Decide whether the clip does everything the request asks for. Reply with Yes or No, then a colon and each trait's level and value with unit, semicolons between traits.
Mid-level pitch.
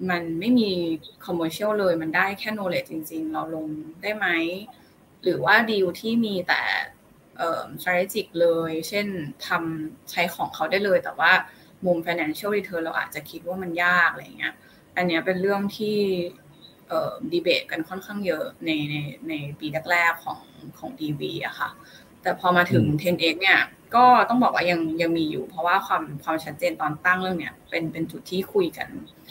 Yes: medium, 175 Hz